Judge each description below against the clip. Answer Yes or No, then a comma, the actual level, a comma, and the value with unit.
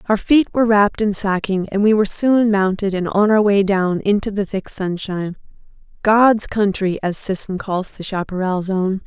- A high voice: Yes, high, 200 Hz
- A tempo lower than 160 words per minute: No, average, 180 wpm